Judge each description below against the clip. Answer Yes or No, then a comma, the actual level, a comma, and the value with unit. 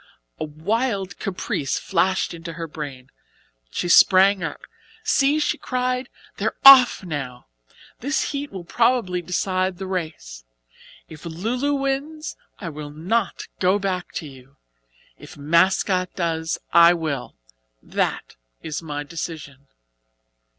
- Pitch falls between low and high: Yes, medium, 180 Hz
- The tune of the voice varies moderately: No, wide, 5.8 semitones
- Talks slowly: Yes, slow, 125 wpm